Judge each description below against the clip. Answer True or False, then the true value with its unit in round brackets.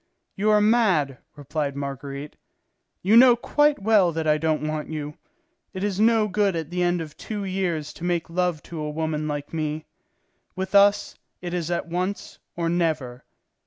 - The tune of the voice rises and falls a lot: False (4.5 semitones)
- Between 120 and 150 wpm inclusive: False (175 wpm)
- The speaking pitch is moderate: True (170 Hz)